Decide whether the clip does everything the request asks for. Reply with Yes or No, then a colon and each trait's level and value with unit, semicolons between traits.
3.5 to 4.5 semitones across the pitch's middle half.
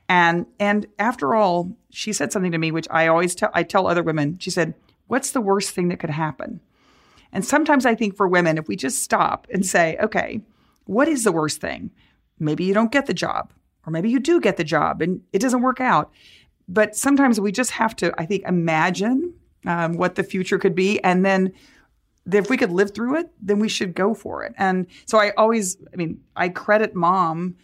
Yes: average, 4.0 semitones